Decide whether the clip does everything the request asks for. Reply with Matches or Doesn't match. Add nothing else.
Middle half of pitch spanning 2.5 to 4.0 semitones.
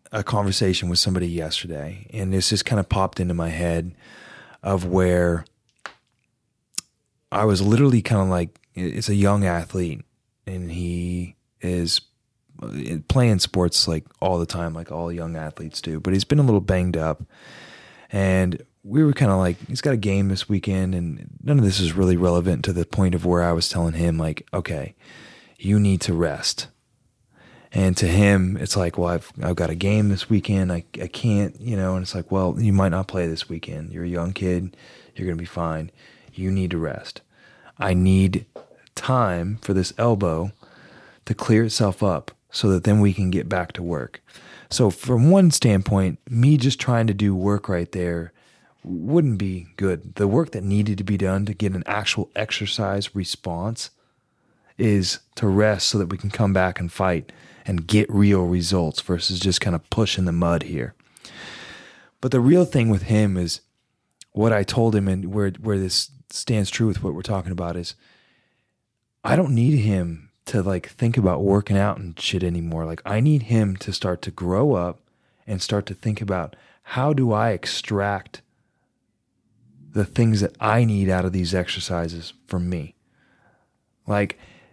Matches